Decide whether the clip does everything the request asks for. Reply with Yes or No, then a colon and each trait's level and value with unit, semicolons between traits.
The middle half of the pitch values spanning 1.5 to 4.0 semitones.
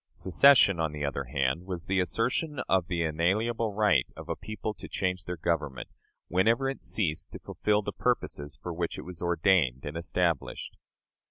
No: average, 4.7 semitones